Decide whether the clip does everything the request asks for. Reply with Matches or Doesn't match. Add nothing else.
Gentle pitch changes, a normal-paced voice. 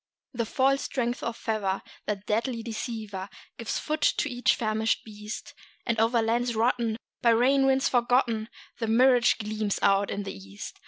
Matches